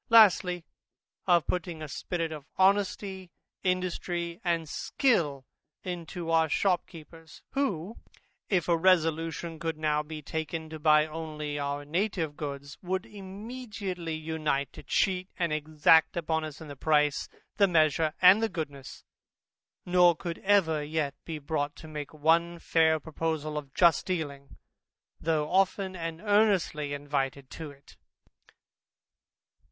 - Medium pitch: Yes, medium, 160 Hz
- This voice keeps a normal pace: No, slow, 130 wpm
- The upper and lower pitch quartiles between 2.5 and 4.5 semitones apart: Yes, average, 3.0 semitones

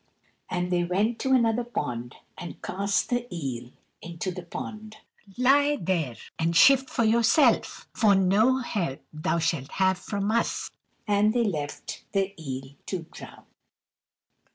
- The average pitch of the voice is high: Yes, high, 195 Hz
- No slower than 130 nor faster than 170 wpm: Yes, average, 140 wpm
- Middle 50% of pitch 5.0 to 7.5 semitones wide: Yes, wide, 5.5 semitones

